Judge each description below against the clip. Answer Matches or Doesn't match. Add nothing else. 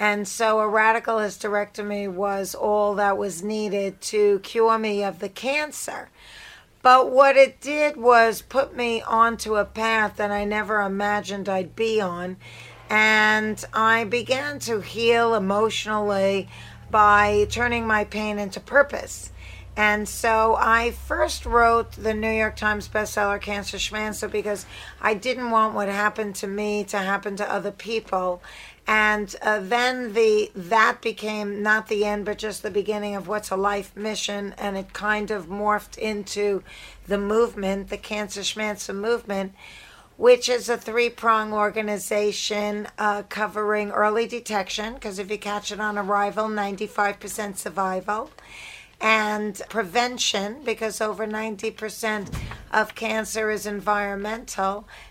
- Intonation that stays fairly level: Matches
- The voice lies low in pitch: Doesn't match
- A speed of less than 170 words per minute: Matches